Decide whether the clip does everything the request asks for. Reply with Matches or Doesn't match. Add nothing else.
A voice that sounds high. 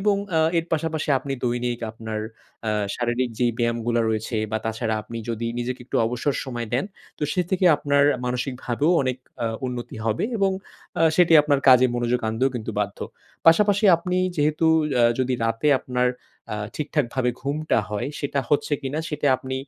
Doesn't match